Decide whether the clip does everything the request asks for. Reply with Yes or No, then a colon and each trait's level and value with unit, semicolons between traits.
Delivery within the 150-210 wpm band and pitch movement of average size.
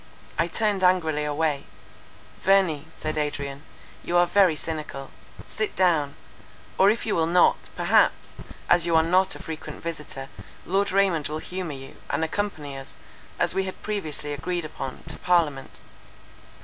Yes: average, 155 wpm; average, 3.9 semitones